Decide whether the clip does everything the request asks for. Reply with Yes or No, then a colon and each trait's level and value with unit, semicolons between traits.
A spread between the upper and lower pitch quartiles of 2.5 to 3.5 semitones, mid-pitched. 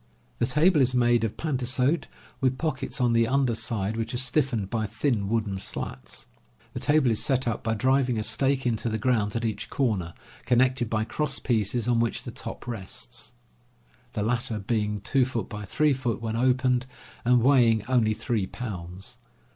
No: average, 2.9 semitones; low, 120 Hz